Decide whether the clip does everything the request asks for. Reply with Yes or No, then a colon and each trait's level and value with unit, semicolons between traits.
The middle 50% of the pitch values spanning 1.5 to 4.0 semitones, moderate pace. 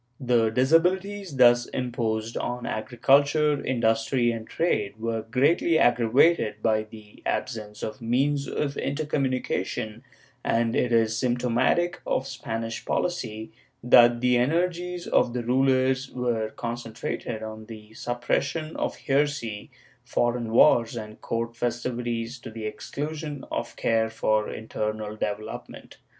No: average, 3.3 semitones; slow, 125 wpm